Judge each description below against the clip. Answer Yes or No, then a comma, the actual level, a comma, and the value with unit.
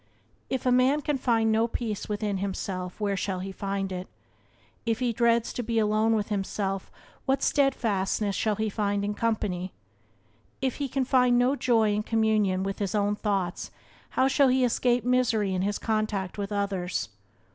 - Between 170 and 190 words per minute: Yes, average, 175 wpm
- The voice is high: Yes, high, 215 Hz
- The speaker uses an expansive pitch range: No, average, 3.5 semitones